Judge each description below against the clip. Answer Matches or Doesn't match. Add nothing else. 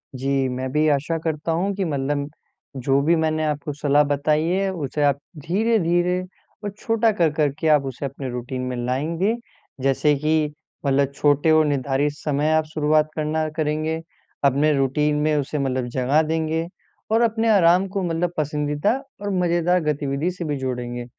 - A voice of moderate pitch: Matches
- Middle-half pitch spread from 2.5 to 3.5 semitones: Matches